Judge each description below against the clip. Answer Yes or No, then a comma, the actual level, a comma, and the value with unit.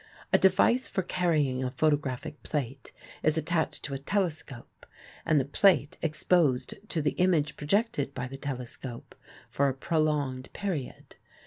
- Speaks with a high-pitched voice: No, medium, 150 Hz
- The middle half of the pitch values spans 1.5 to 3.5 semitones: No, average, 3.9 semitones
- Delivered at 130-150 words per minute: Yes, average, 140 wpm